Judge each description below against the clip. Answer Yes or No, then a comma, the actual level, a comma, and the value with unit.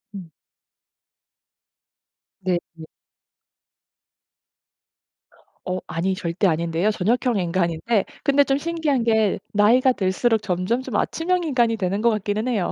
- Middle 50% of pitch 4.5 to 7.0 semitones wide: Yes, average, 5.3 semitones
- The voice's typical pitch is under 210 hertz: No, high, 215 Hz